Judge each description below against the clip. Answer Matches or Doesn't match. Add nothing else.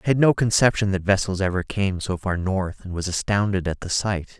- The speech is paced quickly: Matches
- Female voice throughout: Doesn't match